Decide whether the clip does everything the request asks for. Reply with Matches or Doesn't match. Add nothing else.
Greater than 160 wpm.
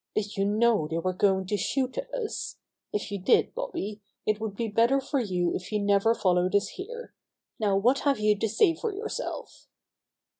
Matches